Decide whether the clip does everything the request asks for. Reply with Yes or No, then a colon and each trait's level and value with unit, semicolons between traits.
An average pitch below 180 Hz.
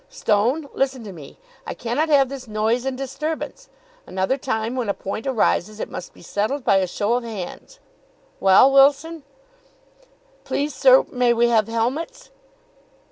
No: high, 245 Hz